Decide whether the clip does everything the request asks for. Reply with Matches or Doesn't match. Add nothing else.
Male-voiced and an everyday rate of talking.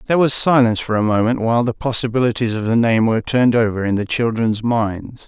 Doesn't match